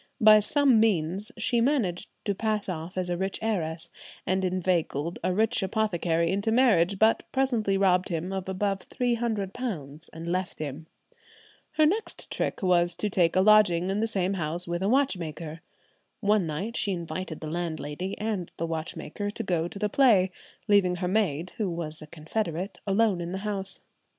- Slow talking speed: No, average, 170 wpm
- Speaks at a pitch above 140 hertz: Yes, high, 190 Hz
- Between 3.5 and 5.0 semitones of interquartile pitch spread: Yes, average, 4.0 semitones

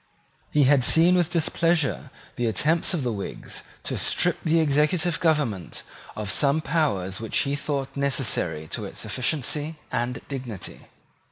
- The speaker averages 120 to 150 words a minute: Yes, average, 145 wpm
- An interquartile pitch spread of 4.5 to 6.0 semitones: Yes, average, 5.1 semitones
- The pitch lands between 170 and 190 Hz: No, medium, 145 Hz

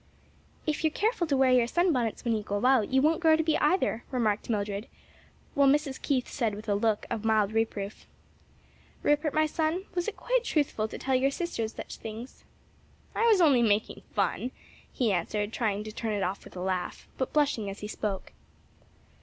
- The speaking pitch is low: No, high, 240 Hz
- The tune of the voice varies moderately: No, wide, 6.2 semitones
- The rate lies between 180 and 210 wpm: Yes, average, 195 wpm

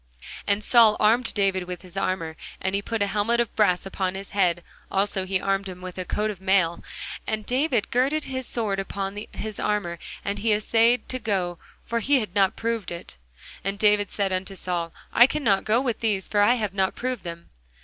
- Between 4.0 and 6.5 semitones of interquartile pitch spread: No, average, 3.1 semitones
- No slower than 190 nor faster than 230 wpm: Yes, fast, 205 wpm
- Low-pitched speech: No, high, 200 Hz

